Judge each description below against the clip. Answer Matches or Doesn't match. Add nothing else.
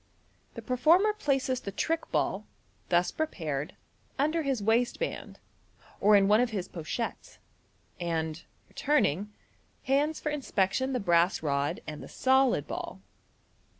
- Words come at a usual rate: Doesn't match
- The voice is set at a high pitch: Matches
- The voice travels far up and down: Matches